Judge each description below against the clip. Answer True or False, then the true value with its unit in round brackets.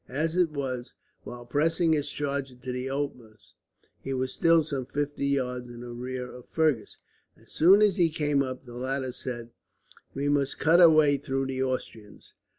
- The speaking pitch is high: False (135 Hz)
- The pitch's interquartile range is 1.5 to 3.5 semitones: True (2.9 semitones)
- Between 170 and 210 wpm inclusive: True (175 wpm)